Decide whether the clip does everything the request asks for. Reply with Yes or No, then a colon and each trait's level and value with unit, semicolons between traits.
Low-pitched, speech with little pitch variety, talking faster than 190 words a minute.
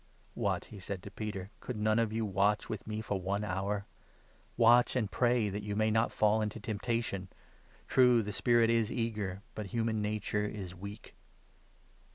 Yes: low, 105 Hz; narrow, 2.0 semitones; average, 200 wpm